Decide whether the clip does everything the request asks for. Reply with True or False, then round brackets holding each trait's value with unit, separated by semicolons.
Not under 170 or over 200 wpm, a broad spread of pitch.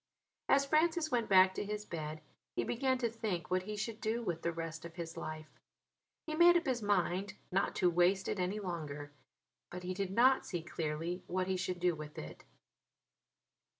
False (190 wpm; 4.8 semitones)